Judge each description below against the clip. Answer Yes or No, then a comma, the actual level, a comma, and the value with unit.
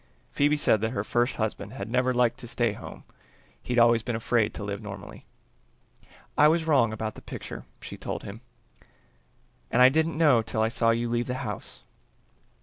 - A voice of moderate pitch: No, low, 120 Hz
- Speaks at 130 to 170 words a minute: No, average, 185 wpm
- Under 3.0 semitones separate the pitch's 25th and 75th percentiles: Yes, narrow, 2.6 semitones